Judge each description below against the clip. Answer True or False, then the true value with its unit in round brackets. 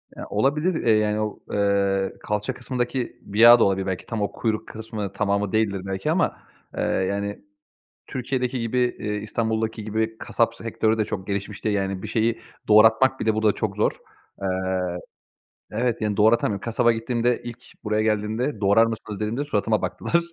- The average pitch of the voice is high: False (110 Hz)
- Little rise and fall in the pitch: True (2.2 semitones)